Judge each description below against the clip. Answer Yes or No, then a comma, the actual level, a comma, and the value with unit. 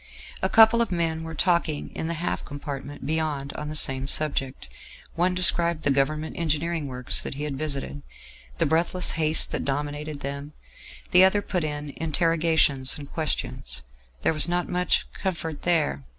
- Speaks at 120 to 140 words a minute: No, average, 165 wpm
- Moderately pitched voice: Yes, medium, 155 Hz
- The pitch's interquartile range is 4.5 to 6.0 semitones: No, average, 2.9 semitones